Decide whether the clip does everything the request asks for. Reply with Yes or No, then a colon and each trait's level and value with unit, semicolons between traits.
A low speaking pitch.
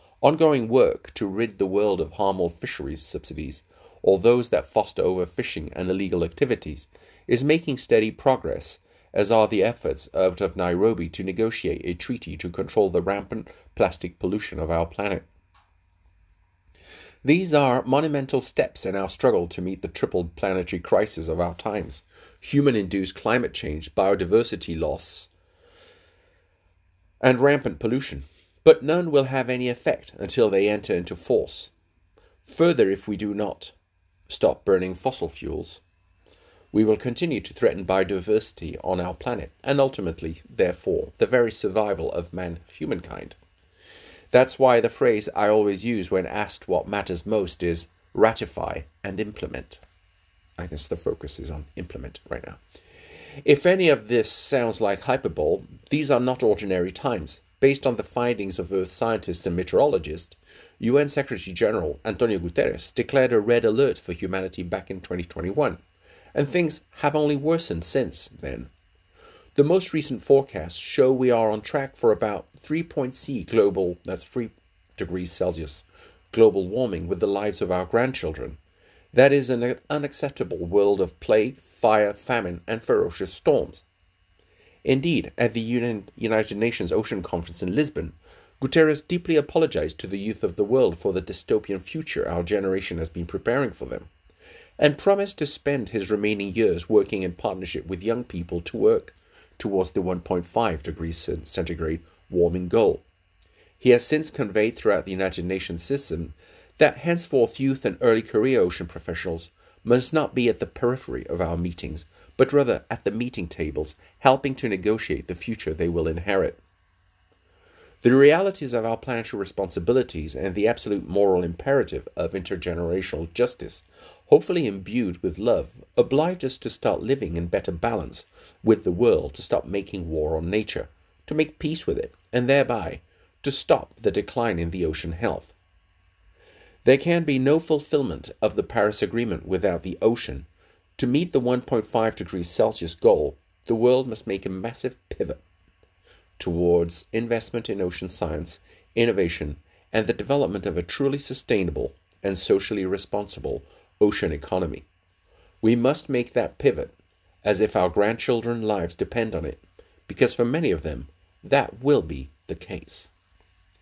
Yes: low, 100 Hz